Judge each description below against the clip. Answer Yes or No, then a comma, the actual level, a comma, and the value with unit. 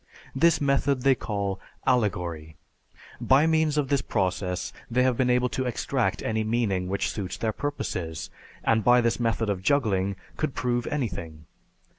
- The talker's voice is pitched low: Yes, low, 115 Hz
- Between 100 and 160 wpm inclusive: Yes, average, 155 wpm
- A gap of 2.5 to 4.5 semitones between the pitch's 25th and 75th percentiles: No, wide, 5.4 semitones